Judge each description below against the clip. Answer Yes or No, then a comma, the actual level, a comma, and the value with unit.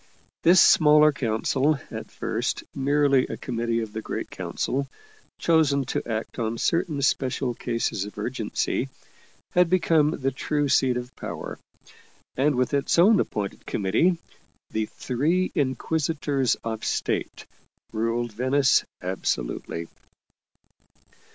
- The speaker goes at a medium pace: No, slow, 120 wpm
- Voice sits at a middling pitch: No, low, 130 Hz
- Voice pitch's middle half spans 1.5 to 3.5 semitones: No, average, 4.5 semitones